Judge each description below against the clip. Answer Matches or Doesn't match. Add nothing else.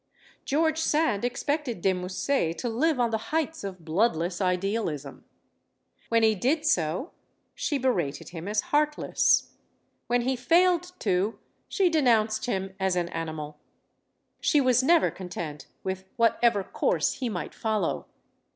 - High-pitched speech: Matches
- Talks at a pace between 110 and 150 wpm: Matches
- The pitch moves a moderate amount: Doesn't match